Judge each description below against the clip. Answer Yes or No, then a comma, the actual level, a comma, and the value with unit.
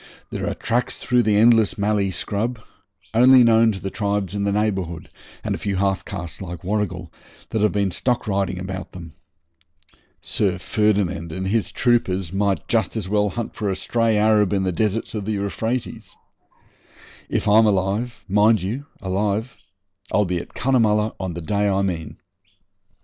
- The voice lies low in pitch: Yes, low, 100 Hz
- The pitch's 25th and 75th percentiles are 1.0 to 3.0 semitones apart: Yes, narrow, 2.6 semitones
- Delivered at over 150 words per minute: Yes, average, 170 wpm